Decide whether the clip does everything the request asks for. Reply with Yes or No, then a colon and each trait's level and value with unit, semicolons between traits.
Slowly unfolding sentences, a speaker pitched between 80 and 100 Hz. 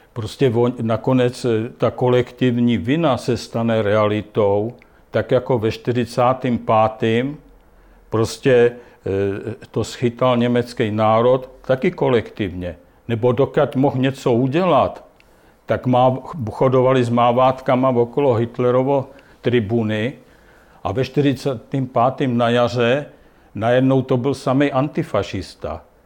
No: slow, 95 wpm; low, 125 Hz